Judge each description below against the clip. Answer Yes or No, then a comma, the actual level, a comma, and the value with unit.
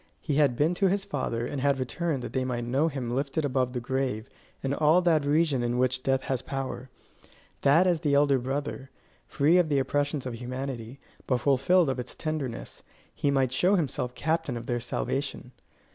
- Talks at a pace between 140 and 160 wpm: No, average, 190 wpm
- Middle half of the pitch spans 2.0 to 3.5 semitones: Yes, average, 2.8 semitones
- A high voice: No, low, 135 Hz